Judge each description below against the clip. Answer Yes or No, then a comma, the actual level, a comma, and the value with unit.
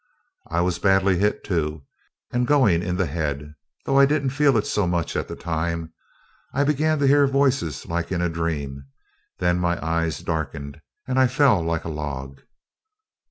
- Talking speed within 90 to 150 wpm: No, average, 175 wpm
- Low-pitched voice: Yes, very low, 85 Hz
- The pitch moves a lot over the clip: Yes, wide, 8.1 semitones